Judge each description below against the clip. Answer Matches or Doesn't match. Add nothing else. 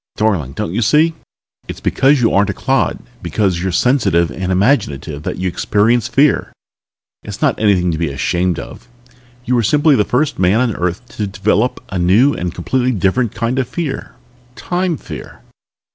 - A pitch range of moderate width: Doesn't match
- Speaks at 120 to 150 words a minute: Doesn't match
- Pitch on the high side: Doesn't match